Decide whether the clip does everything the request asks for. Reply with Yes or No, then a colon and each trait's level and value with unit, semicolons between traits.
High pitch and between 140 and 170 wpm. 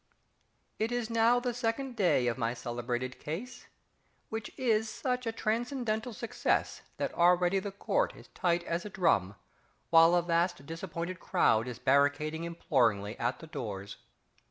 No: medium, 175 Hz; average, 155 wpm